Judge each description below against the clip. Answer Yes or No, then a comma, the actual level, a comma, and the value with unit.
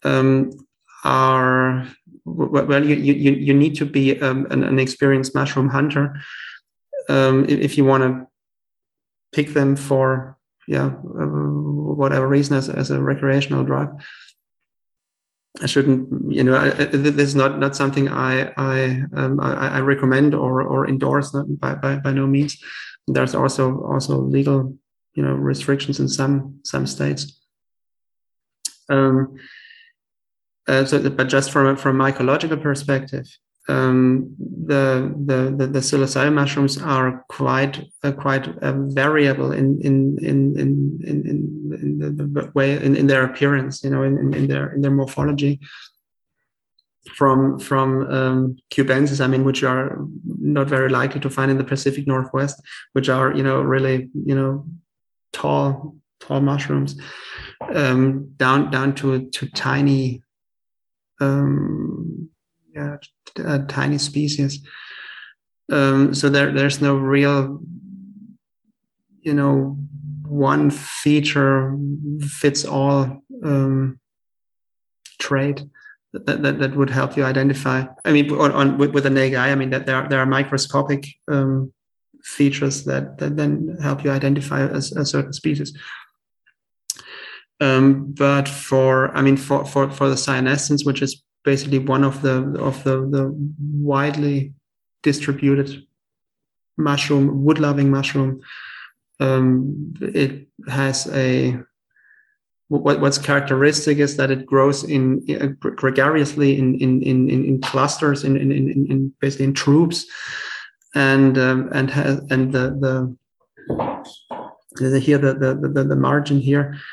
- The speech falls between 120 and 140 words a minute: Yes, slow, 135 wpm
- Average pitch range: No, narrow, 1.2 semitones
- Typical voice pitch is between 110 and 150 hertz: Yes, medium, 140 Hz